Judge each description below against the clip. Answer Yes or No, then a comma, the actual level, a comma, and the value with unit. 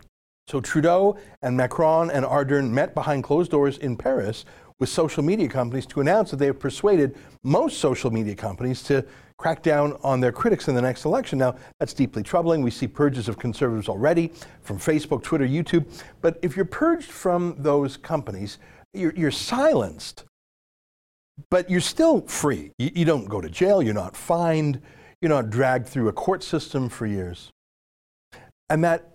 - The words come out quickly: No, average, 175 wpm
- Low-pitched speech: No, medium, 145 Hz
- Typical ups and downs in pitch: Yes, average, 4.7 semitones